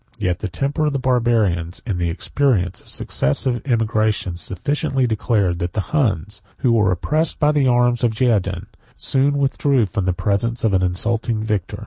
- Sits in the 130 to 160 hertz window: No, low, 110 Hz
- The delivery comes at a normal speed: Yes, average, 175 wpm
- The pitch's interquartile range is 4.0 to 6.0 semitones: Yes, wide, 5.6 semitones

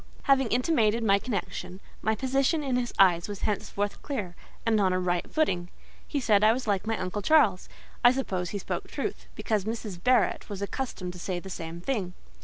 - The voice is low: No, high, 210 Hz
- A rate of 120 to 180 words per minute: No, average, 195 wpm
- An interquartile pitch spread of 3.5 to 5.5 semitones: Yes, average, 5.1 semitones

